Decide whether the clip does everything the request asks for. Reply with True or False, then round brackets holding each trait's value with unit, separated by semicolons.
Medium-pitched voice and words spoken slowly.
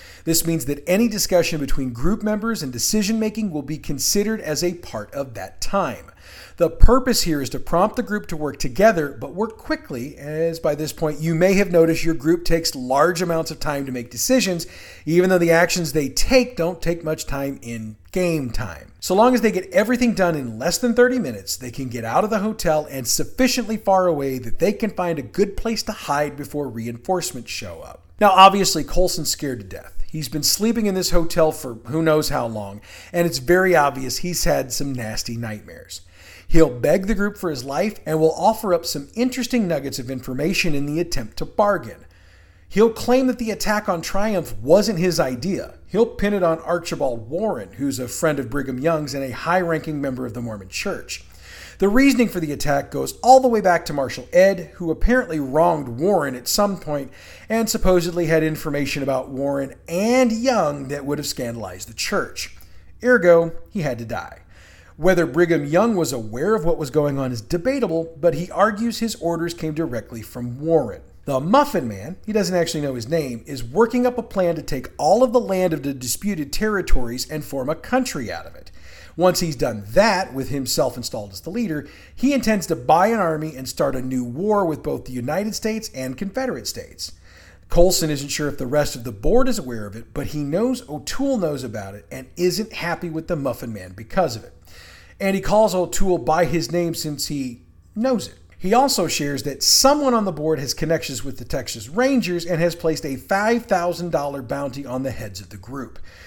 False (160 Hz; 205 wpm)